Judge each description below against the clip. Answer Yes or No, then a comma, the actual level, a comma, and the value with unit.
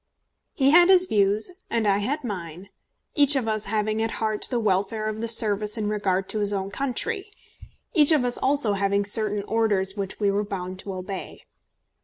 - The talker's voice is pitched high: Yes, high, 215 Hz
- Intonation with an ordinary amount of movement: Yes, average, 3.2 semitones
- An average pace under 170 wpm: No, average, 190 wpm